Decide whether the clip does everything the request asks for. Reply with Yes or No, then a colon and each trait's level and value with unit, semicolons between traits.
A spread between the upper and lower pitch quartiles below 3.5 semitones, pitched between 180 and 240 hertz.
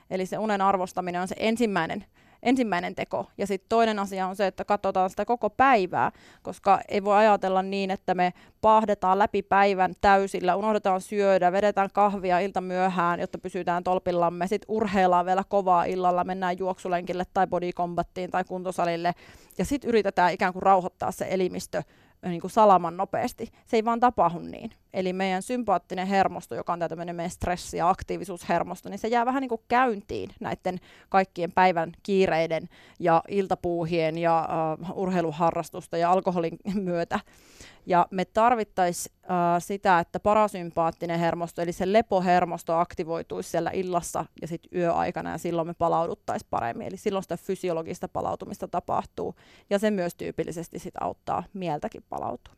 Yes: narrow, 2.4 semitones; medium, 185 Hz